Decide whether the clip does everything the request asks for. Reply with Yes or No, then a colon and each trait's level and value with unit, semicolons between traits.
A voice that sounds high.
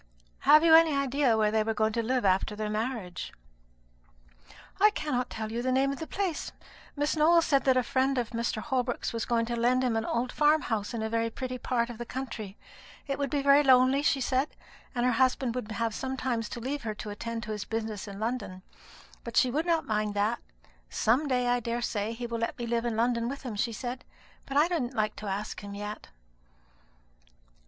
Yes: high, 240 Hz